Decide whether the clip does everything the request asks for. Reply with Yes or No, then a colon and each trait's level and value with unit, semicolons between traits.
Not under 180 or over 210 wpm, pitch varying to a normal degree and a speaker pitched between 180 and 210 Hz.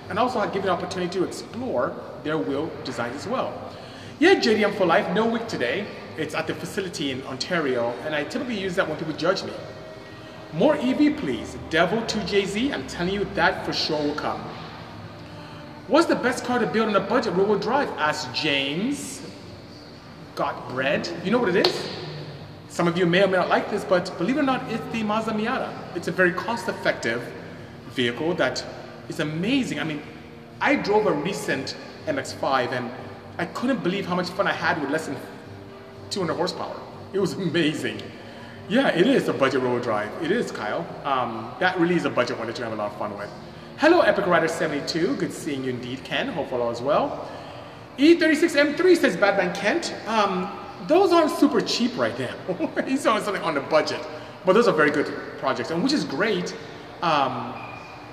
No: average, 190 wpm; wide, 7.5 semitones; medium, 185 Hz